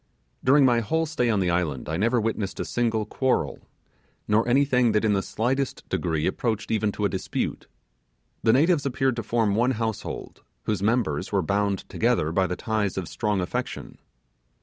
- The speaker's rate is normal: Yes, average, 175 wpm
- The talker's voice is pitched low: Yes, low, 110 Hz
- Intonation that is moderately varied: Yes, average, 3.9 semitones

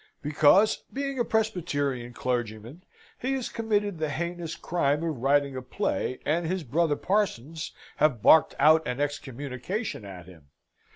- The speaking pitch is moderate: Yes, medium, 150 Hz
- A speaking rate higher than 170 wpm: No, average, 140 wpm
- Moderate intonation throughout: No, wide, 6.1 semitones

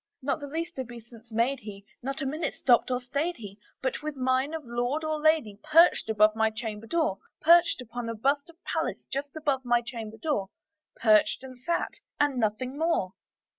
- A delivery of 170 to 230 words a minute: Yes, average, 185 wpm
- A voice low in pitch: No, very high, 255 Hz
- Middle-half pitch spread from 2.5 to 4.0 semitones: No, average, 4.9 semitones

